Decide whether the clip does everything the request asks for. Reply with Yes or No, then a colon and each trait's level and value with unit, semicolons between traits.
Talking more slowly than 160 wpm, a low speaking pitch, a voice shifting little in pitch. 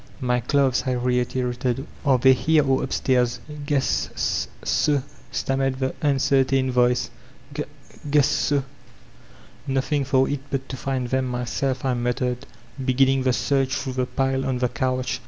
Yes: average, 150 wpm; low, 130 Hz; narrow, 1.4 semitones